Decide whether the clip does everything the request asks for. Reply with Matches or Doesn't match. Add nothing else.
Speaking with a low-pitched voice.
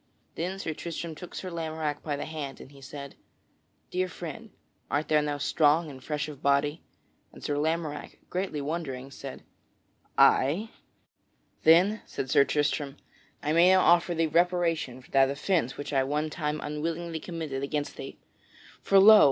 Doesn't match